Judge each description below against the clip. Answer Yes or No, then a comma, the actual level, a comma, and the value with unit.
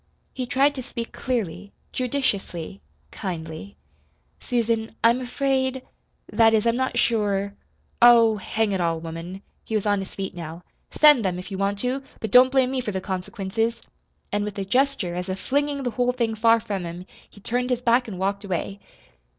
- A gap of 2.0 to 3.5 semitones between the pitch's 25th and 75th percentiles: No, average, 4.5 semitones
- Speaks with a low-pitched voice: No, high, 220 Hz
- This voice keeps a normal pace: Yes, average, 185 wpm